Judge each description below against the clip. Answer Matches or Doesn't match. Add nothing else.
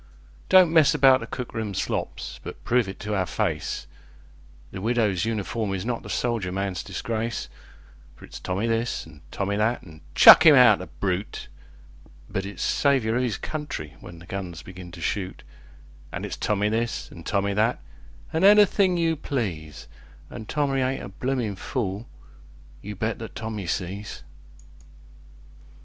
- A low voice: Matches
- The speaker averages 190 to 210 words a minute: Doesn't match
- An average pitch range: Matches